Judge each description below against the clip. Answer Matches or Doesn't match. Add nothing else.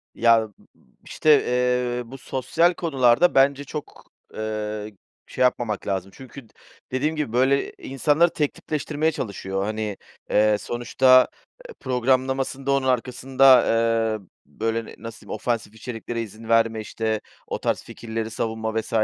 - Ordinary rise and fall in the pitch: Matches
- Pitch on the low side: Matches